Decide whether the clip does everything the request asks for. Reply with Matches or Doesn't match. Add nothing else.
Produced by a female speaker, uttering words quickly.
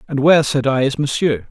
Doesn't match